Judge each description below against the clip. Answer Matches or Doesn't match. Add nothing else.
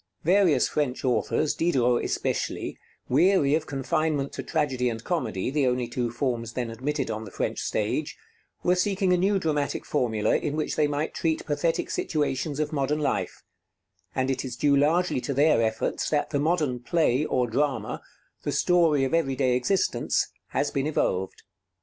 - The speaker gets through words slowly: Doesn't match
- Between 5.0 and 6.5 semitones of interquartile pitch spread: Doesn't match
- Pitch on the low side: Doesn't match